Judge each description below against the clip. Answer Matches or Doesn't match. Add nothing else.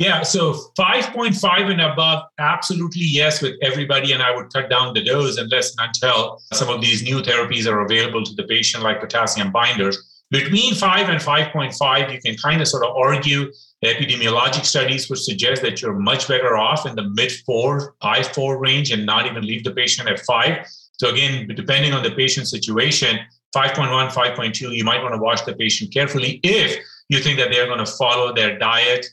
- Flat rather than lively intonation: Doesn't match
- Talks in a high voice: Doesn't match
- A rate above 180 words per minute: Matches